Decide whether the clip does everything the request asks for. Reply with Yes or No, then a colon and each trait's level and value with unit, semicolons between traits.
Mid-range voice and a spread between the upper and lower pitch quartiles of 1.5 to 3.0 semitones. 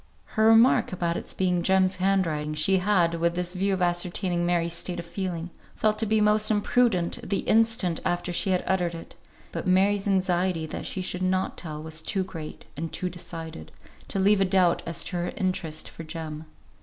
Yes: medium, 180 Hz; narrow, 2.4 semitones